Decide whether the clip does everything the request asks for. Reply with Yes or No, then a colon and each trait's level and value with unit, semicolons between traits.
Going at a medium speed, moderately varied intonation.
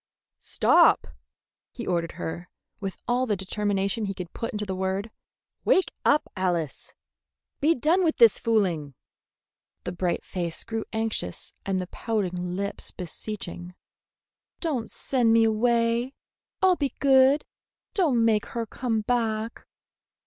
No: slow, 130 wpm; average, 4.5 semitones